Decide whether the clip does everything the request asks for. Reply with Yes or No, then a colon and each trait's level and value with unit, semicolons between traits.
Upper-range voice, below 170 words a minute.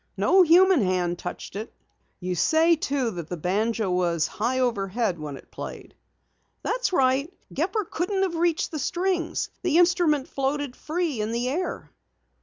Yes: very high, 265 Hz; average, 160 wpm